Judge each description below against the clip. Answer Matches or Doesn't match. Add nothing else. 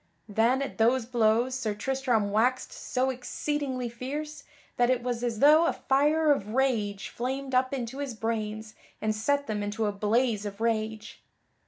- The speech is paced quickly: Doesn't match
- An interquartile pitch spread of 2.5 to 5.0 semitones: Matches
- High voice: Matches